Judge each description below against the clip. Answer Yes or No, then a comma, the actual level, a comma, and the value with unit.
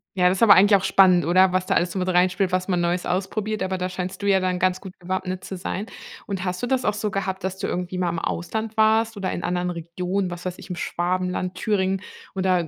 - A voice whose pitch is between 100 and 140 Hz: No, medium, 185 Hz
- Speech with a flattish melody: Yes, narrow, 1.4 semitones